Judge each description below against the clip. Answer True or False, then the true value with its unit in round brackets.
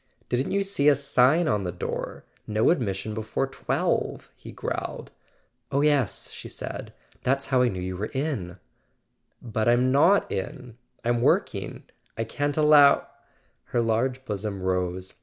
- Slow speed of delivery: False (160 wpm)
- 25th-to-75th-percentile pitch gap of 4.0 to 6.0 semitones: True (5.1 semitones)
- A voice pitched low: True (125 Hz)